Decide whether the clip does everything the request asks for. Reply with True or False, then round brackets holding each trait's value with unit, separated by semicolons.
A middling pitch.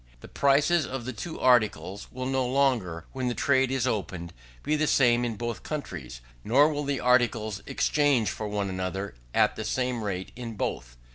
False (120 Hz)